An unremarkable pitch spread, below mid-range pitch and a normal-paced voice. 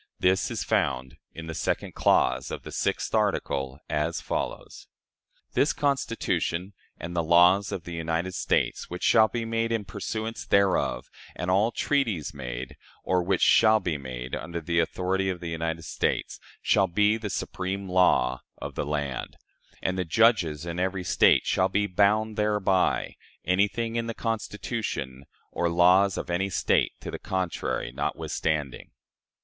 Yes: average, 4.1 semitones; very low, 90 Hz; average, 155 wpm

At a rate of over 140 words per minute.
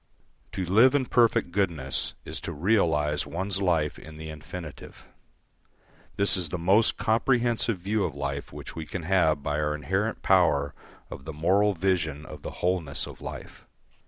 Yes: average, 160 wpm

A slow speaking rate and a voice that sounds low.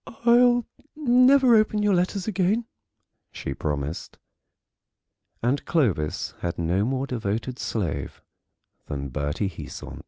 Yes: slow, 105 wpm; low, 130 Hz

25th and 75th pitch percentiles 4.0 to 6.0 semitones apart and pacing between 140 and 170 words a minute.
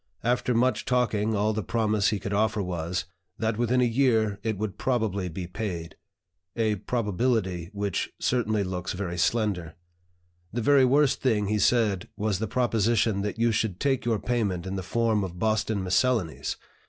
No: average, 3.4 semitones; average, 165 wpm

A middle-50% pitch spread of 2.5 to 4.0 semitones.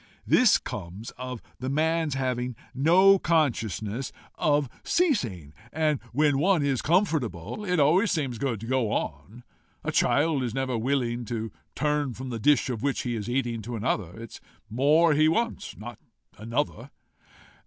No: average, 4.8 semitones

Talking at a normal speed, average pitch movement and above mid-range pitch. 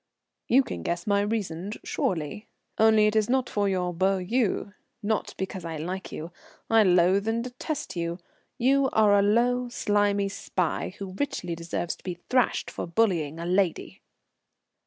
Yes: average, 160 wpm; average, 4.0 semitones; high, 200 Hz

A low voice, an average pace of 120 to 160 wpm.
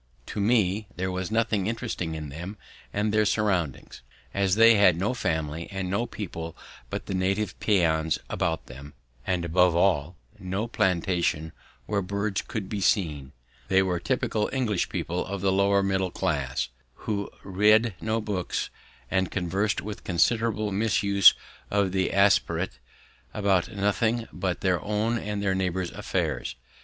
Yes: very low, 95 Hz; average, 150 wpm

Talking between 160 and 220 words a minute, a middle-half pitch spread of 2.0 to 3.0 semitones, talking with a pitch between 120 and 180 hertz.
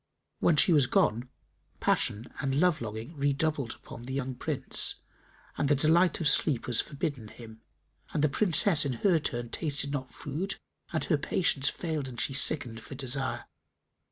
No: average, 165 wpm; average, 3.8 semitones; medium, 140 Hz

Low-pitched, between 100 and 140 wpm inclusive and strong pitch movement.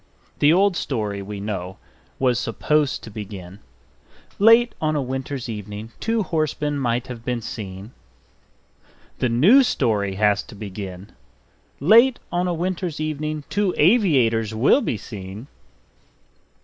Yes: low, 125 Hz; slow, 135 wpm; wide, 7.4 semitones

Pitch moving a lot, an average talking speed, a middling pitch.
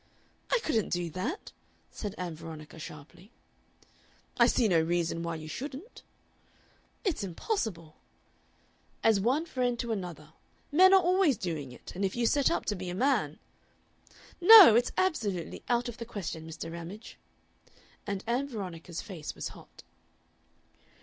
No: wide, 7.0 semitones; average, 150 wpm; high, 200 Hz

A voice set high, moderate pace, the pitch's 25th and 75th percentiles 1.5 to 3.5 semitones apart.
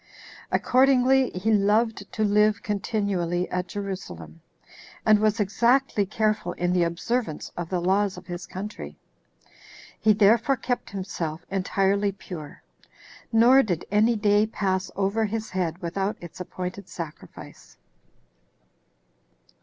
No: high, 200 Hz; slow, 120 wpm; average, 3.2 semitones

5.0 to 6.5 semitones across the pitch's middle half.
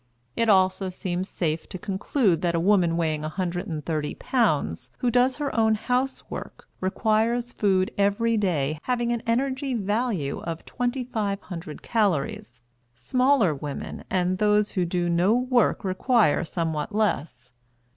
Yes: wide, 5.6 semitones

